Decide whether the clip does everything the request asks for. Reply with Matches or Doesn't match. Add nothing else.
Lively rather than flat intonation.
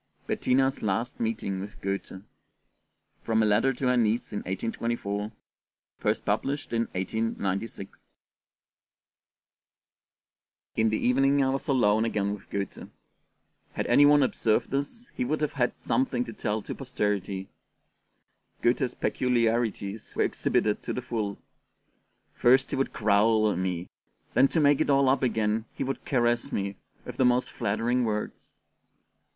Doesn't match